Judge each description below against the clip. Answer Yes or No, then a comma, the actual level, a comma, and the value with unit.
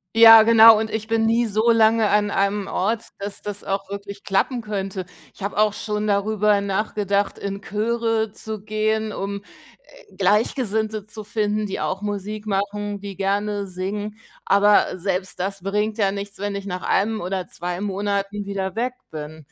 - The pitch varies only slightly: Yes, narrow, 1.6 semitones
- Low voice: No, high, 205 Hz